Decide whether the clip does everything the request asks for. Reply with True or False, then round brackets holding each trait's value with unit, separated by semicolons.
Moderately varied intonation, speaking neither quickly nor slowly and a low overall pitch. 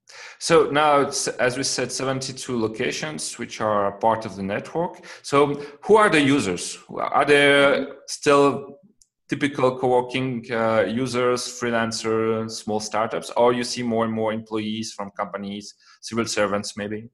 True (4.1 semitones; 150 wpm; 120 Hz)